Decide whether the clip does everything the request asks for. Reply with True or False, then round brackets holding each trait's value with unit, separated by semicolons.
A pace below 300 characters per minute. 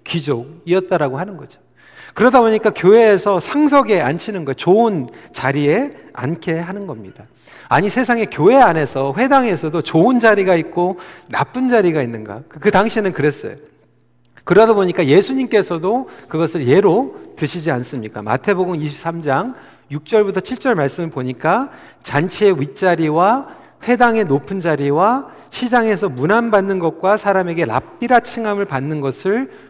False (320 characters per minute)